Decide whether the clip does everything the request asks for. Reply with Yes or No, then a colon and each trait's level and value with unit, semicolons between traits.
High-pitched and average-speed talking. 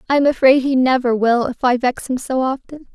No: very high, 260 Hz; fast, 245 wpm